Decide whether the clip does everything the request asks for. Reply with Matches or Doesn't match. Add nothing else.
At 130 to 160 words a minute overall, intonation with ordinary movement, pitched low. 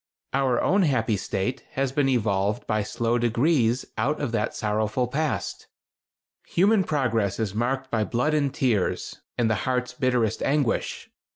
Matches